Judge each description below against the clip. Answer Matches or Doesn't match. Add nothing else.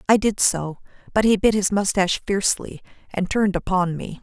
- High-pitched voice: Matches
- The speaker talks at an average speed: Matches